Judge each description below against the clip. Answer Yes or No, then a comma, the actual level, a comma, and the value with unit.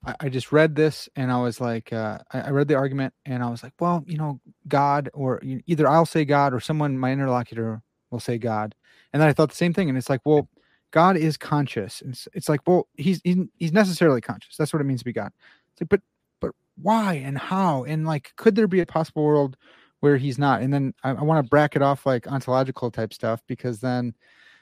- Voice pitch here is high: No, medium, 140 Hz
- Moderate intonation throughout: Yes, average, 3.8 semitones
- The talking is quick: Yes, fast, 230 wpm